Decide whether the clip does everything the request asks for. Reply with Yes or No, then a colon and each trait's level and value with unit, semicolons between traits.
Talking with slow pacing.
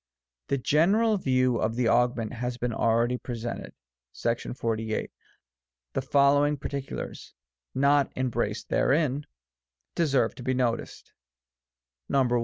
Yes: slow, 110 wpm